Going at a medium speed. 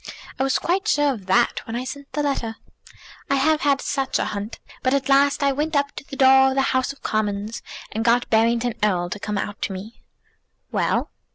No: fast, 215 wpm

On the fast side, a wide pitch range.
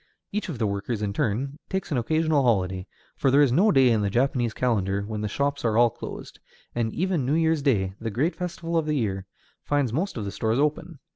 Yes: fast, 225 wpm; wide, 6.2 semitones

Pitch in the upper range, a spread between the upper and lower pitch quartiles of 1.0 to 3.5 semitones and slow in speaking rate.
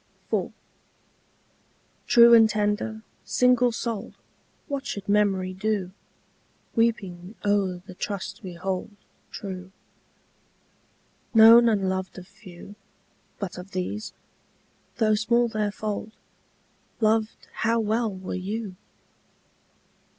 Yes: high, 210 Hz; average, 3.0 semitones; slow, 100 wpm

